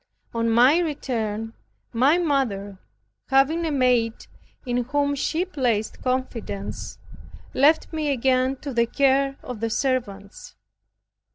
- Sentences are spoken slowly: Yes, slow, 110 wpm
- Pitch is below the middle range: No, very high, 255 Hz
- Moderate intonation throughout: Yes, average, 3.7 semitones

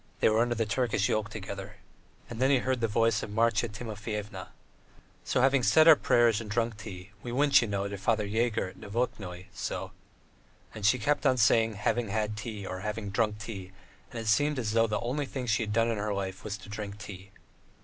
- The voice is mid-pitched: No, low, 110 Hz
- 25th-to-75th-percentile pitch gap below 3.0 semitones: Yes, narrow, 2.4 semitones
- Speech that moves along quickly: Yes, fast, 220 wpm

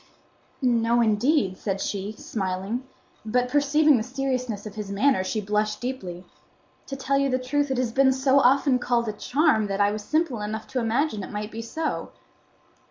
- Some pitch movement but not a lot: Yes, average, 4.4 semitones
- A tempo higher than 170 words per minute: Yes, average, 180 wpm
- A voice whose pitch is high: Yes, high, 235 Hz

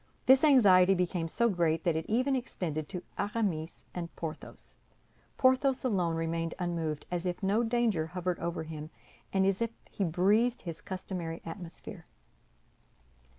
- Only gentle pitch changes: No, average, 4.8 semitones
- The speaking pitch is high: No, medium, 180 Hz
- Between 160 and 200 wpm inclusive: No, average, 145 wpm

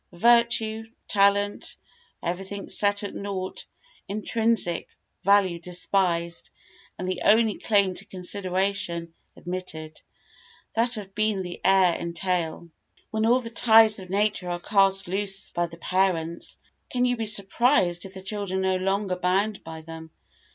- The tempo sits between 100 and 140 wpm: Yes, slow, 135 wpm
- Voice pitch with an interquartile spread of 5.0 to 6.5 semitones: No, average, 2.9 semitones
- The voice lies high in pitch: Yes, high, 195 Hz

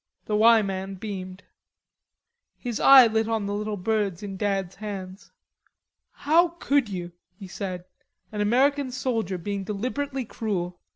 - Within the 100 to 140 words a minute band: Yes, slow, 135 wpm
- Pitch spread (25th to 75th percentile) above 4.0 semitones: No, average, 3.5 semitones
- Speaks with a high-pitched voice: Yes, high, 210 Hz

